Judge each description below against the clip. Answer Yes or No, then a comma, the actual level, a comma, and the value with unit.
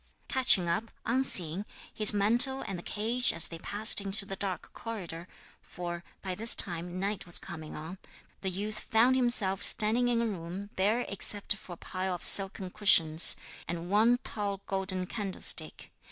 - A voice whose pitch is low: No, high, 195 Hz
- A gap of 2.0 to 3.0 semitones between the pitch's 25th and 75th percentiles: No, average, 3.5 semitones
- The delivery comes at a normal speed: Yes, average, 165 wpm